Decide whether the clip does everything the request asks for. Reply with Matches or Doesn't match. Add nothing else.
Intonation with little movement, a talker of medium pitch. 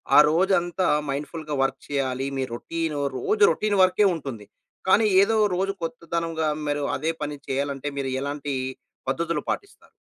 Doesn't match